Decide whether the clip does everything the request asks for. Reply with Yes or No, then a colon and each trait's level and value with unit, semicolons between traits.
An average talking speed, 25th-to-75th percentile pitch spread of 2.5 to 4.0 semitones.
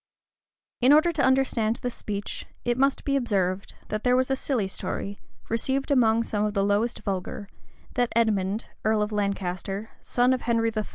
Yes: average, 180 wpm; average, 3.7 semitones